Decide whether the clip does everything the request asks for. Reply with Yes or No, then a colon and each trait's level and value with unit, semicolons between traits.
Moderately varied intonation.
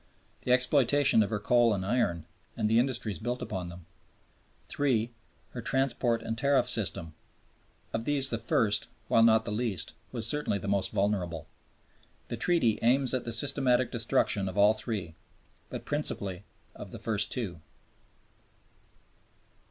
Yes: average, 3.8 semitones